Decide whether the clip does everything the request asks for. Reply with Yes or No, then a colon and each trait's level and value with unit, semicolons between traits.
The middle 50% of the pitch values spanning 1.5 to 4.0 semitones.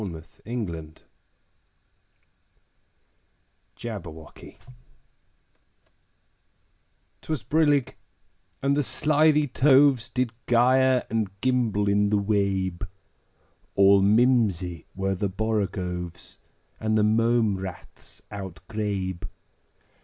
No: average, 4.5 semitones